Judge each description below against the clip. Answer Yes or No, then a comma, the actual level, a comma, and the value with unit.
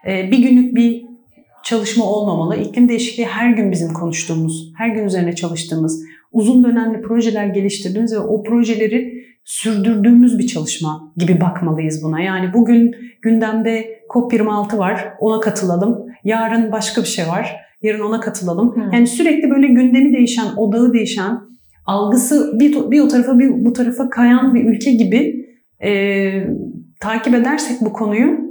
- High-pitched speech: Yes, high, 225 Hz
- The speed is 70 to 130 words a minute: No, fast, 140 wpm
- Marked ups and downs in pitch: No, average, 3.1 semitones